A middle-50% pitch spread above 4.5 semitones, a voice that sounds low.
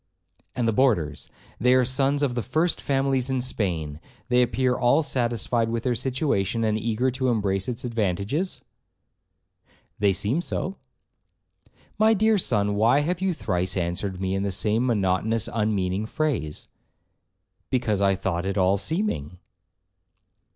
Yes: average, 5.1 semitones; low, 115 Hz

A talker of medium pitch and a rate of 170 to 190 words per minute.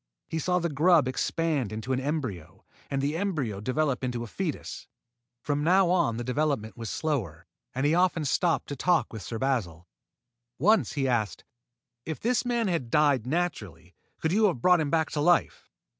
Yes: medium, 145 Hz; average, 180 wpm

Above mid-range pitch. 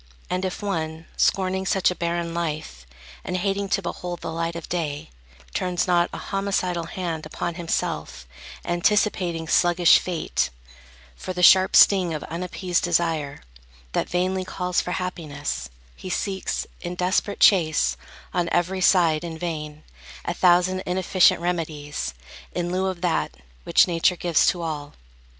No: medium, 175 Hz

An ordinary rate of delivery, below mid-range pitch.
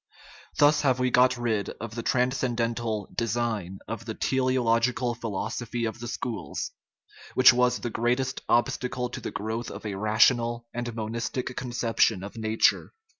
Yes: average, 150 wpm; low, 120 Hz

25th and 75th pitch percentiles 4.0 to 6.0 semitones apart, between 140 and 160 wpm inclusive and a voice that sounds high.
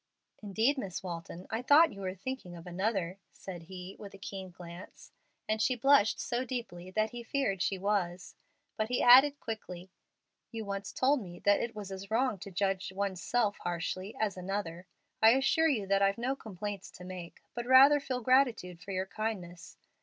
No: average, 4.4 semitones; average, 185 wpm; high, 200 Hz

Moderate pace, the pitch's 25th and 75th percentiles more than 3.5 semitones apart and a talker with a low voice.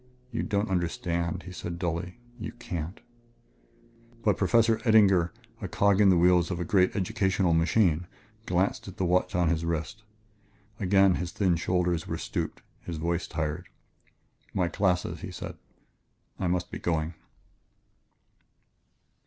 No: average, 145 wpm; narrow, 2.5 semitones; very low, 90 Hz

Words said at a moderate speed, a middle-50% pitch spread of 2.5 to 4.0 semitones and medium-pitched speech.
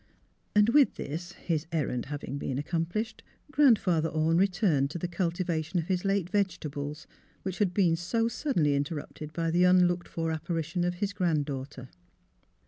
Yes: average, 175 wpm; average, 3.4 semitones; medium, 170 Hz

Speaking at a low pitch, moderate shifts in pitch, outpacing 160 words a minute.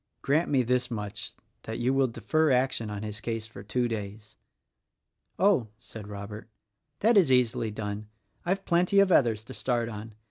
Yes: low, 115 Hz; average, 3.9 semitones; average, 170 wpm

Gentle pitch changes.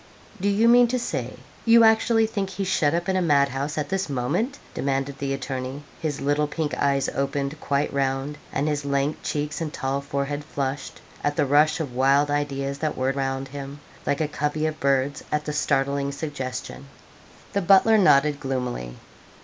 Yes: narrow, 2.3 semitones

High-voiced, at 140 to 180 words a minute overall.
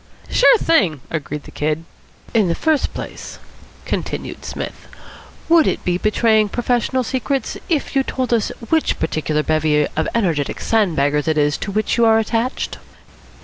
Yes: high, 215 Hz; average, 150 wpm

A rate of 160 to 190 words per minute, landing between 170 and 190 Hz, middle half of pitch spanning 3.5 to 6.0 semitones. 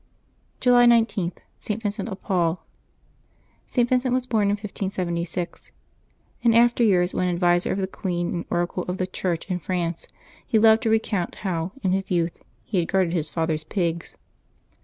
Yes: average, 165 wpm; medium, 185 Hz; average, 4.0 semitones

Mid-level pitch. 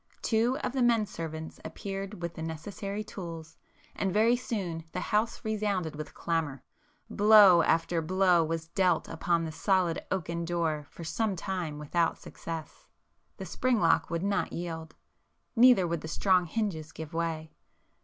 Yes: medium, 175 Hz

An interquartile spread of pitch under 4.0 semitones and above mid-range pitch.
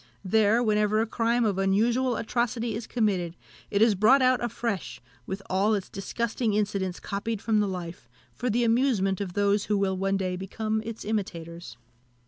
Yes: average, 3.0 semitones; high, 210 Hz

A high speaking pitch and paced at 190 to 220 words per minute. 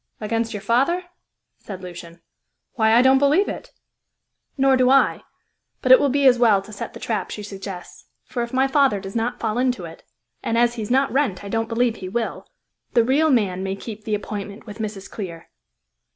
Yes: high, 225 Hz; fast, 205 wpm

